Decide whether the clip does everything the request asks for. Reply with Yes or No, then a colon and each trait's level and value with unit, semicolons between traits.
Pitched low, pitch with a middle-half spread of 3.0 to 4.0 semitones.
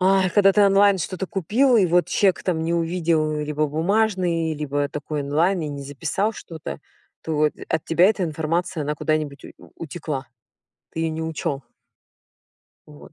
No: medium, 165 Hz; average, 3.7 semitones